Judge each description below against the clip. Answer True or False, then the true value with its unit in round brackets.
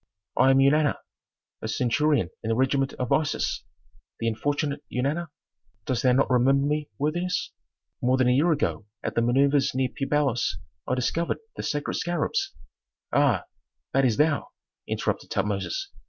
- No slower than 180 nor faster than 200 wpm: False (155 wpm)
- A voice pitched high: False (135 Hz)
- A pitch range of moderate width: True (3.1 semitones)